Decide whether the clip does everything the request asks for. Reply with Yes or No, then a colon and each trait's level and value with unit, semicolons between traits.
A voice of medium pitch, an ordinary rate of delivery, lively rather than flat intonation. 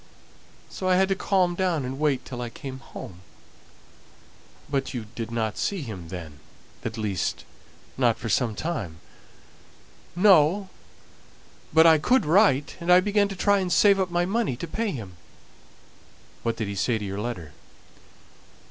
Yes: medium, 145 Hz; average, 155 wpm; wide, 8.8 semitones